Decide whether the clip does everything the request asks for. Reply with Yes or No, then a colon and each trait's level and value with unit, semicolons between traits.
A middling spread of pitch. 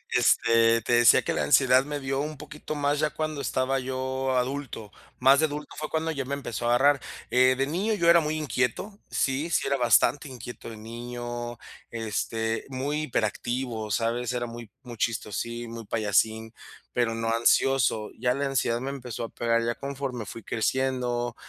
Yes: average, 3.1 semitones